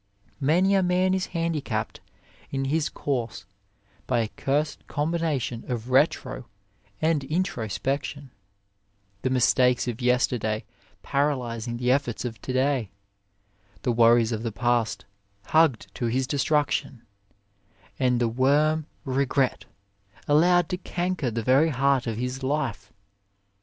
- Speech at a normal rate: No, slow, 130 wpm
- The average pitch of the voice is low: Yes, low, 130 Hz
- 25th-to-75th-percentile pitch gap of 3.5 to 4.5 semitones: Yes, average, 3.9 semitones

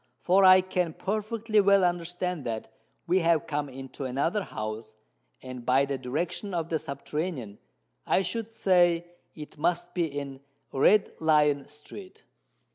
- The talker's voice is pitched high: No, medium, 165 Hz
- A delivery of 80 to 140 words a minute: Yes, slow, 135 wpm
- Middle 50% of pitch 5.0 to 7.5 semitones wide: Yes, average, 5.3 semitones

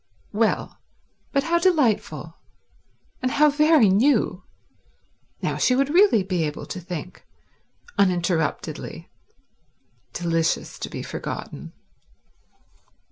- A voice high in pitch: Yes, high, 220 Hz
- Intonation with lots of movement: Yes, wide, 8.8 semitones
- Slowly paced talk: Yes, slow, 95 wpm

